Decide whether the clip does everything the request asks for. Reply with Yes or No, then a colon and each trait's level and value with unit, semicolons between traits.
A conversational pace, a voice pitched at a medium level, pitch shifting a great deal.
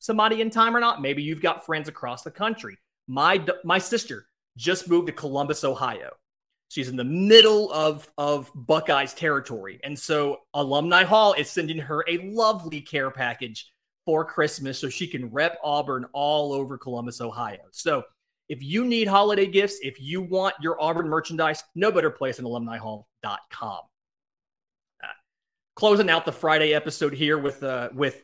No: average, 165 wpm; medium, 155 Hz; average, 5.0 semitones